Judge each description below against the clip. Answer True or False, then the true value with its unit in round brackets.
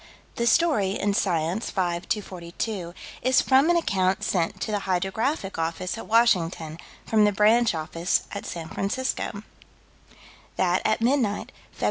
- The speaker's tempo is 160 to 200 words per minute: False (140 wpm)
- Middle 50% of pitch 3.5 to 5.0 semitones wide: True (4.4 semitones)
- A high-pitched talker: True (200 Hz)